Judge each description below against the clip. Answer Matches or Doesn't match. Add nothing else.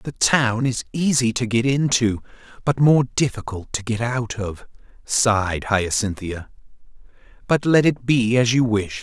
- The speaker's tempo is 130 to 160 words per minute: Matches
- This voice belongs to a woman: Doesn't match